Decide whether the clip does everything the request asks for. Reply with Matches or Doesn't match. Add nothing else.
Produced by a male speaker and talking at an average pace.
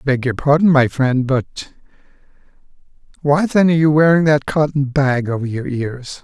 Matches